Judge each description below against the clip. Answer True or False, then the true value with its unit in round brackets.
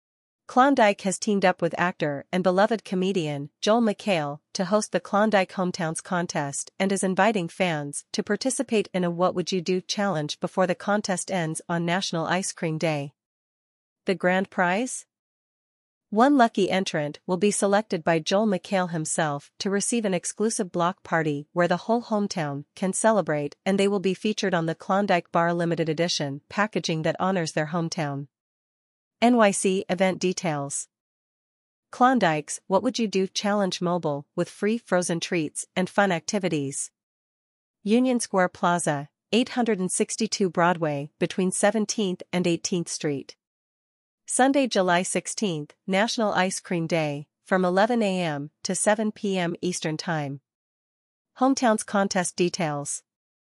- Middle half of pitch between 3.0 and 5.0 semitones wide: True (3.5 semitones)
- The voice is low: False (185 Hz)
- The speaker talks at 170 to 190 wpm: False (140 wpm)